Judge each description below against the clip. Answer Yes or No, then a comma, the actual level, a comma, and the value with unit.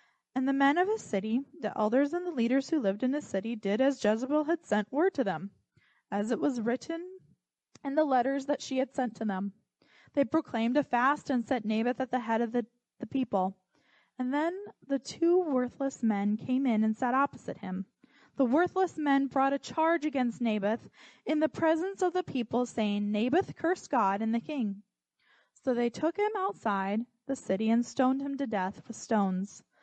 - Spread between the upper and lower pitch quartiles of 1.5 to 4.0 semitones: No, average, 4.7 semitones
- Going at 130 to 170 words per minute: No, average, 195 wpm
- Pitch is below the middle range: No, very high, 255 Hz